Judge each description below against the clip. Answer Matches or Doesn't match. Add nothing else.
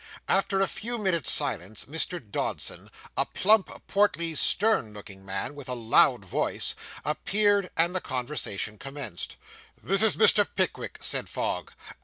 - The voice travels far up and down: Matches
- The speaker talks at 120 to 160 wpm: Matches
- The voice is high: Doesn't match